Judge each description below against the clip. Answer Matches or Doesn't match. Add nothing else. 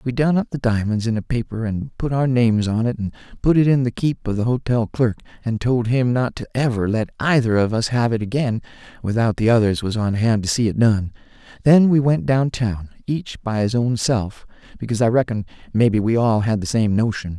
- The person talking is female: Doesn't match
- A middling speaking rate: Doesn't match